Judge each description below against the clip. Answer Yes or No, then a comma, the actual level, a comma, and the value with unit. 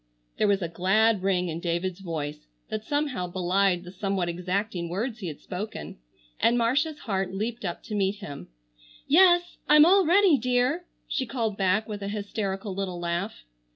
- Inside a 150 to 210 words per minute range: Yes, average, 170 wpm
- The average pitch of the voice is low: No, high, 200 Hz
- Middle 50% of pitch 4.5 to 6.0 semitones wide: Yes, average, 4.8 semitones